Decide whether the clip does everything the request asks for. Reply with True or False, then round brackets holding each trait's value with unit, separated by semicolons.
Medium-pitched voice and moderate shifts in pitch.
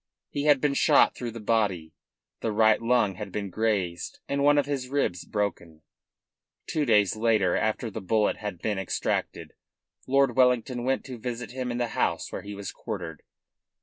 False (110 Hz; 3.9 semitones)